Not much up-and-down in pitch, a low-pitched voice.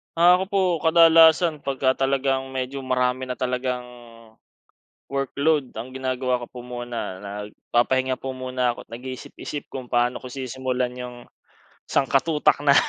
Yes: narrow, 1.7 semitones; low, 130 Hz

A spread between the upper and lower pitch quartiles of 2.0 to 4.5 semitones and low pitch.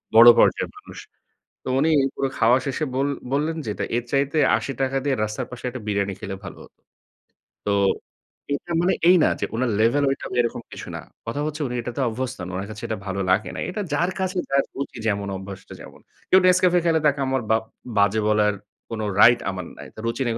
No: average, 5.0 semitones; low, 120 Hz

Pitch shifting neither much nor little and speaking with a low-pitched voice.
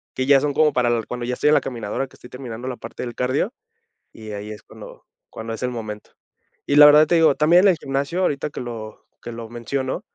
Yes: average, 4.0 semitones; low, 125 Hz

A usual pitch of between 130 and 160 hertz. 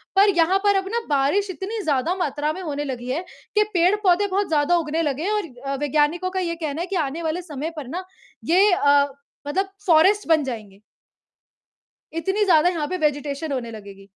No: very high, 325 Hz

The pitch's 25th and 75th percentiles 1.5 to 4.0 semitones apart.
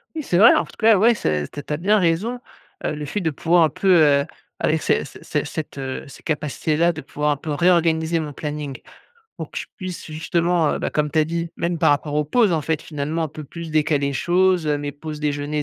Yes: average, 2.8 semitones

